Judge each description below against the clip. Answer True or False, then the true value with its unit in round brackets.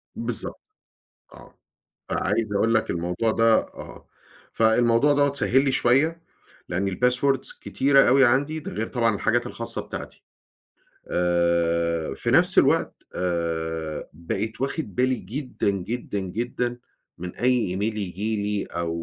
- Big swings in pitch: True (6.0 semitones)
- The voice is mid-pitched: False (110 Hz)